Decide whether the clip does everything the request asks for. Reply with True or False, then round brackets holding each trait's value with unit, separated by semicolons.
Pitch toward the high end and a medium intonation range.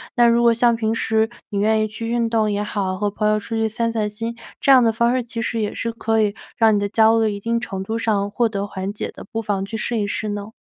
False (220 Hz; 1.9 semitones)